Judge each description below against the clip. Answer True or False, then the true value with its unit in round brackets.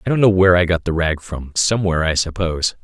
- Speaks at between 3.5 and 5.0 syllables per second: False (6.8 syllables/s)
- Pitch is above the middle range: False (90 Hz)